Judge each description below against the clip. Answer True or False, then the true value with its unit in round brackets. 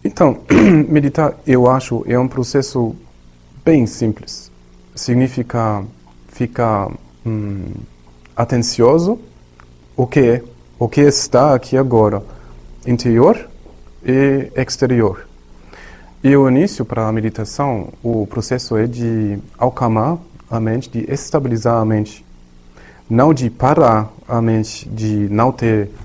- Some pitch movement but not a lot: True (4.3 semitones)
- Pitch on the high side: False (115 Hz)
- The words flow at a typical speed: False (115 wpm)